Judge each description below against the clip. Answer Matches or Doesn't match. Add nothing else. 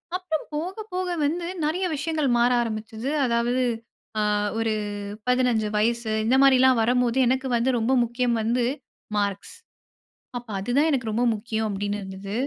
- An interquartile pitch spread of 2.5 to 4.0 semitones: Matches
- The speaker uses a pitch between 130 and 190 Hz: Doesn't match